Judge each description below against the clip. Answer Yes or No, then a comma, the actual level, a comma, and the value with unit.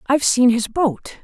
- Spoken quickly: No, average, 195 wpm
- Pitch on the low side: No, very high, 255 Hz